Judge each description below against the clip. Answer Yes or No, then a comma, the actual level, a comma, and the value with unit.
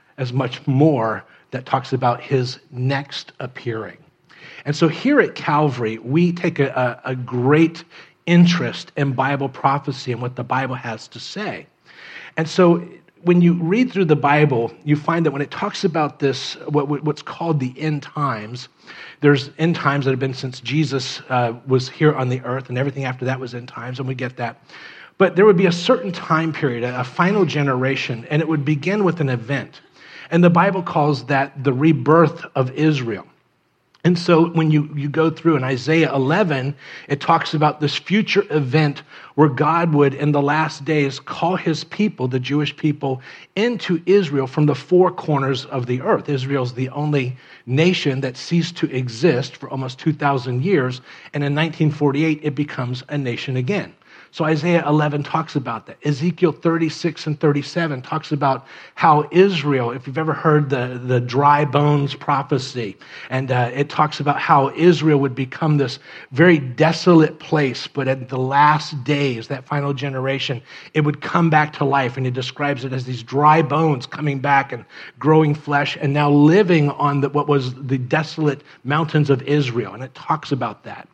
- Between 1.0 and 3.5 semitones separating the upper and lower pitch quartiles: Yes, average, 3.1 semitones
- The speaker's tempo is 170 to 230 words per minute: Yes, average, 180 wpm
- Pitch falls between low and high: Yes, medium, 145 Hz